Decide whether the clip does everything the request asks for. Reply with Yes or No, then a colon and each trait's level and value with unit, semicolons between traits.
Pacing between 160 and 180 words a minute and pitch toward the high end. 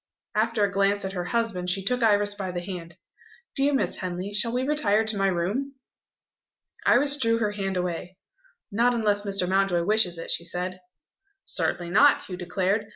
Yes: average, 175 wpm; high, 200 Hz